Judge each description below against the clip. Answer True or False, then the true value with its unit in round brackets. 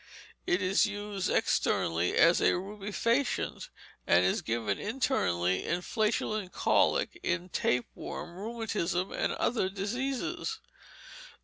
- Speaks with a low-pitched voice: False (195 Hz)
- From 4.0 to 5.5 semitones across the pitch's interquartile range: True (4.7 semitones)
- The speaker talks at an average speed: False (105 wpm)